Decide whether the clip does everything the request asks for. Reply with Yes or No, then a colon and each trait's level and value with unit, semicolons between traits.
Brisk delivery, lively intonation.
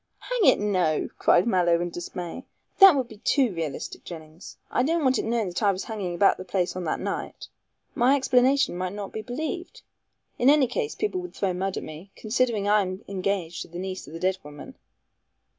Yes: fast, 210 wpm; wide, 6.2 semitones